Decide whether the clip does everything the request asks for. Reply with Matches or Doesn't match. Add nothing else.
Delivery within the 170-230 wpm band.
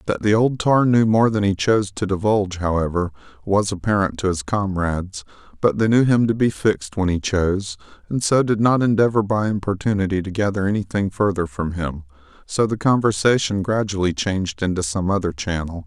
Matches